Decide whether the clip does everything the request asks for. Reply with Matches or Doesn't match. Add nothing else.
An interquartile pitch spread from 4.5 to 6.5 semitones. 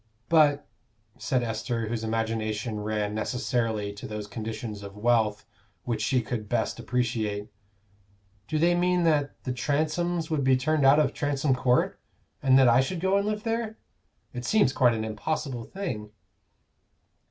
Matches